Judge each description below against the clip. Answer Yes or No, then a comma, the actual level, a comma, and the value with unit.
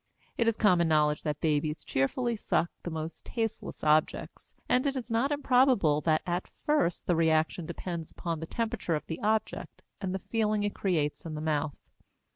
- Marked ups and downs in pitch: Yes, wide, 6.1 semitones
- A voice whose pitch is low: No, medium, 175 Hz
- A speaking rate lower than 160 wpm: No, average, 180 wpm